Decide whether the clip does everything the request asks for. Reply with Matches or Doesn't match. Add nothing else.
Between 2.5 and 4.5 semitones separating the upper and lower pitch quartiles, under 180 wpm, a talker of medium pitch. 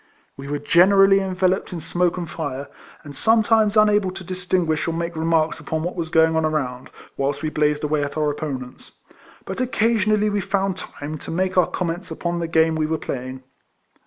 Doesn't match